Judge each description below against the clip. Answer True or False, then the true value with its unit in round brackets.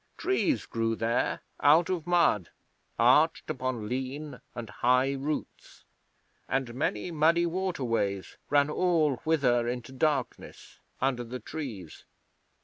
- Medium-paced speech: False (115 wpm)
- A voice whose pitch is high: False (135 Hz)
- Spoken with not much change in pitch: False (4.8 semitones)